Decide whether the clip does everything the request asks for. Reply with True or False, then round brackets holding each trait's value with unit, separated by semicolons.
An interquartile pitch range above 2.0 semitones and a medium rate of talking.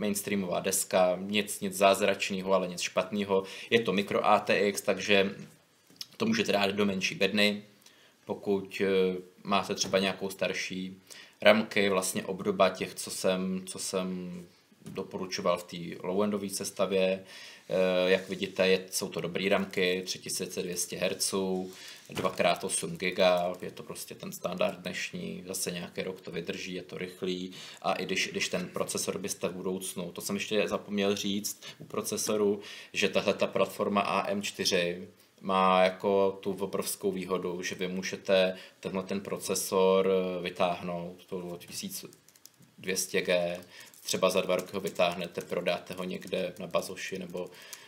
False (1.2 semitones; 140 wpm)